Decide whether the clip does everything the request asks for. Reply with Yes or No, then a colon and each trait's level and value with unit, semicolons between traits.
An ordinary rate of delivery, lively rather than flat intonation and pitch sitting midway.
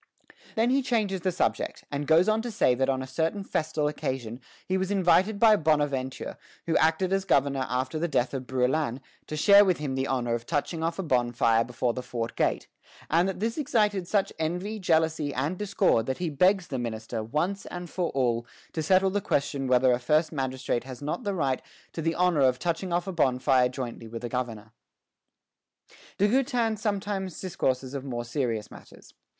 Yes: average, 190 wpm; wide, 6.7 semitones; medium, 150 Hz